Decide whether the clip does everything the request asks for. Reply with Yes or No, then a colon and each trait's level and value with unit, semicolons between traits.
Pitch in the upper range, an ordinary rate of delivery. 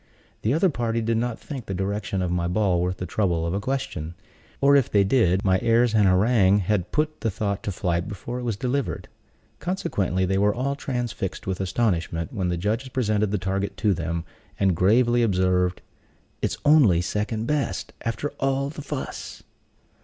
No: low, 105 Hz; average, 185 wpm